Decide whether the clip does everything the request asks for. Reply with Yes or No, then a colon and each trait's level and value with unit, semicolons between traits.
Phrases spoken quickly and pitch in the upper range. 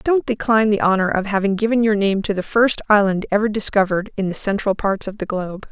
Yes: fast, 230 wpm; high, 205 Hz